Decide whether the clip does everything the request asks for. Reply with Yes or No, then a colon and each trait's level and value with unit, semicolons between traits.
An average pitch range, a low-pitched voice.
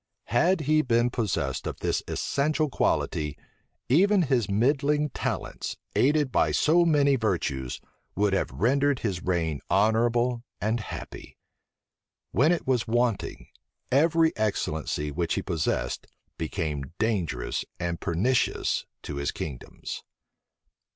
No: wide, 8.6 semitones; low, 115 Hz